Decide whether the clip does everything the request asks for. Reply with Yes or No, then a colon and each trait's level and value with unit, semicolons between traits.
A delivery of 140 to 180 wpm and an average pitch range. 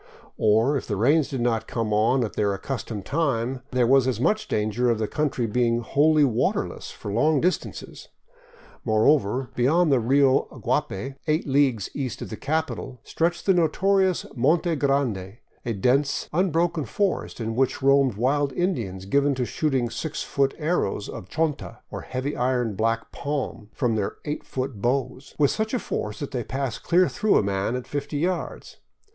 Yes: average, 170 wpm; average, 4.6 semitones